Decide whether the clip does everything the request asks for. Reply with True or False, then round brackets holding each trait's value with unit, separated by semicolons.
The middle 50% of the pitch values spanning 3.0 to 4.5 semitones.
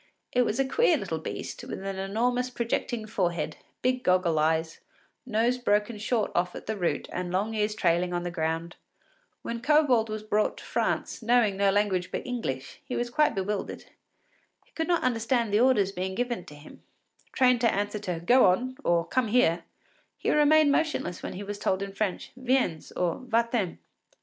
False (5.3 semitones)